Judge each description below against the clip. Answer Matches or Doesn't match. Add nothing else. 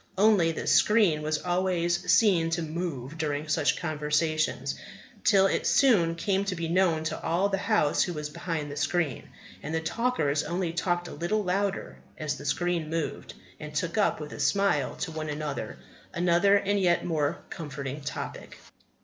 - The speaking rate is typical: Matches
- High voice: Doesn't match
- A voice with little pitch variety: Doesn't match